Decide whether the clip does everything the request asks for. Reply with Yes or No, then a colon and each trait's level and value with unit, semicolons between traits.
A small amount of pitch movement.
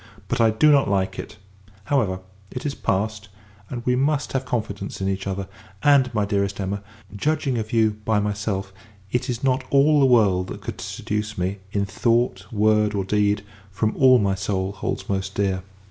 No: average, 4.1 semitones